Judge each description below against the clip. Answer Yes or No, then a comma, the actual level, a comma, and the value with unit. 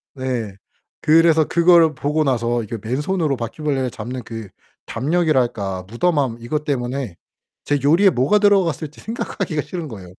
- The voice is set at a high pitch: No, medium, 140 Hz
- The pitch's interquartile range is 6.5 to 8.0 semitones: No, average, 5.3 semitones